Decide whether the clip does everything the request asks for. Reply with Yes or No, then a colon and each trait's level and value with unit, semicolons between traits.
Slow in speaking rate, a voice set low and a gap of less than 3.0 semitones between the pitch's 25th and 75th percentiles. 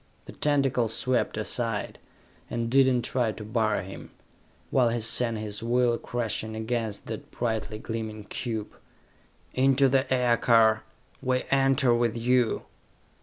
Yes: slow, 130 wpm; low, 120 Hz; narrow, 2.5 semitones